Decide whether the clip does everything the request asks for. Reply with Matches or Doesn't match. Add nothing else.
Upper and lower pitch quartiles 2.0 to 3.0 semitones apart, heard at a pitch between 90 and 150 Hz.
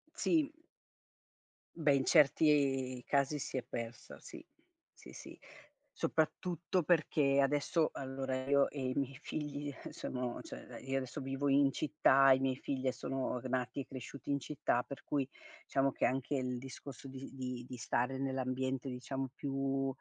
Doesn't match